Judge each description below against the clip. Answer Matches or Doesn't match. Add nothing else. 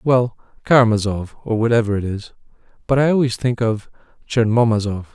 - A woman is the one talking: Doesn't match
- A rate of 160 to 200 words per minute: Doesn't match